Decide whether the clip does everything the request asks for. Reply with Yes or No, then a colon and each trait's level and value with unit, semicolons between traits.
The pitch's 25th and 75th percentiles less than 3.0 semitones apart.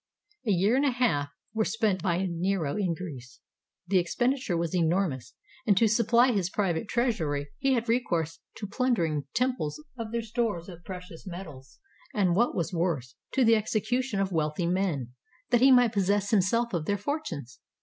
No: wide, 5.5 semitones